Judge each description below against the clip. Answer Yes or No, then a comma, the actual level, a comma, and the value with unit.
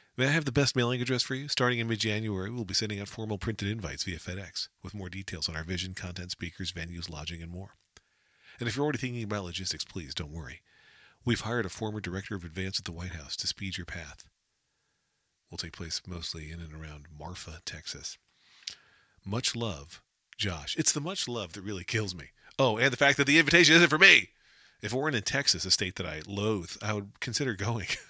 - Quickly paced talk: Yes, fast, 220 wpm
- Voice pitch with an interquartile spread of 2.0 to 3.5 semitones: No, average, 5.2 semitones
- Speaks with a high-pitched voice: No, low, 100 Hz